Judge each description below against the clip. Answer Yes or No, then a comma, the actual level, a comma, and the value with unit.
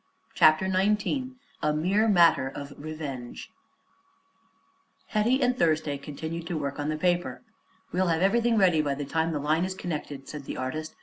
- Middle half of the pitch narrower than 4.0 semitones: No, average, 4.3 semitones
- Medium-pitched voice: Yes, medium, 160 Hz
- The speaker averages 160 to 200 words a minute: Yes, average, 165 wpm